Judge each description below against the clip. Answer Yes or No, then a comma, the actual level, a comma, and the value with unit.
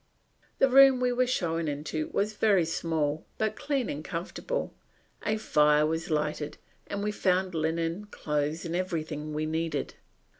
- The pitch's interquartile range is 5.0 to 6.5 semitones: Yes, average, 5.3 semitones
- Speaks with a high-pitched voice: No, medium, 165 Hz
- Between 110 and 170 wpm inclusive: Yes, average, 150 wpm